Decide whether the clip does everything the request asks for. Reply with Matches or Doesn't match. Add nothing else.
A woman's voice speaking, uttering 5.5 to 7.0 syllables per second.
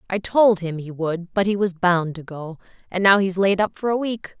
Doesn't match